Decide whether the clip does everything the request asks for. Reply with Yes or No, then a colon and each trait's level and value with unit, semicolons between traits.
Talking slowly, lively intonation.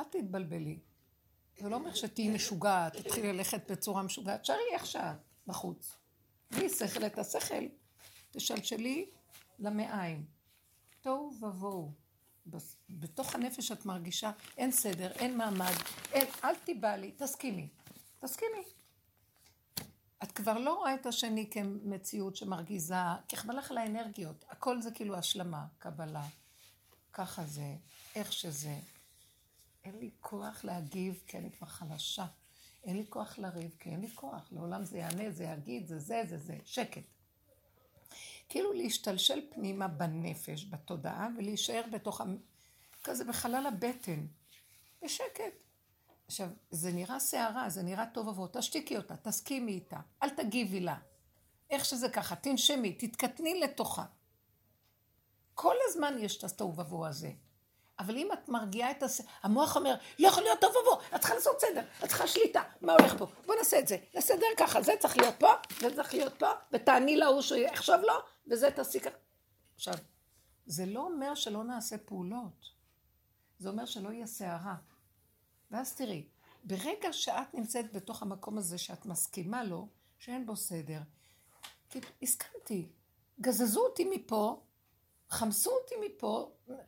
No: average, 140 wpm; wide, 6.5 semitones